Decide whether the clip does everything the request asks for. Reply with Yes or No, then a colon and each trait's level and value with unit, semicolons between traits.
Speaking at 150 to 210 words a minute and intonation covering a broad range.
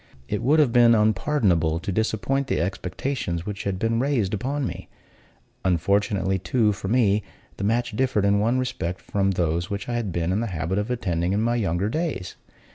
No: average, 190 wpm; average, 4.4 semitones